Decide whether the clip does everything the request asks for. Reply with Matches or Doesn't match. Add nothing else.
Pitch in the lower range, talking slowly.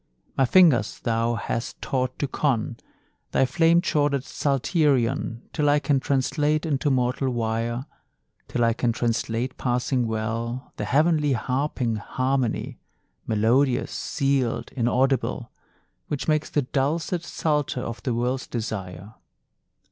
Matches